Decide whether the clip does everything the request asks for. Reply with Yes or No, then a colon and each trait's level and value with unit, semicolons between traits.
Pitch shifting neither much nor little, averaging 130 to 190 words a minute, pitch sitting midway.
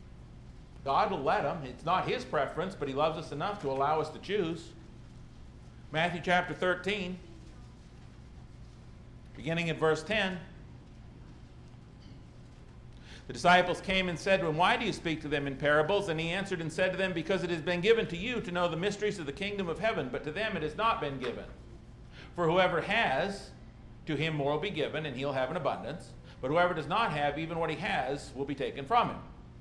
No: average, 4.0 semitones; average, 200 wpm; medium, 170 Hz